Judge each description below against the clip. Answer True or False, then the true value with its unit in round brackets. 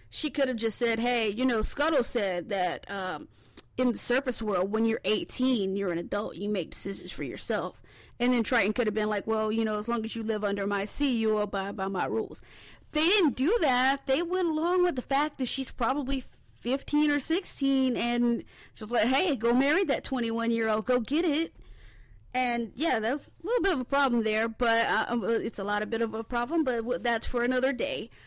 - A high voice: True (240 Hz)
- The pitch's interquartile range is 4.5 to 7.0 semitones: False (3.8 semitones)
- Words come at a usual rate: False (225 wpm)